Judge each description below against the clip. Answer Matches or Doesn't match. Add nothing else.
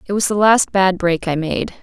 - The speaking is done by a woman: Matches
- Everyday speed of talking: Doesn't match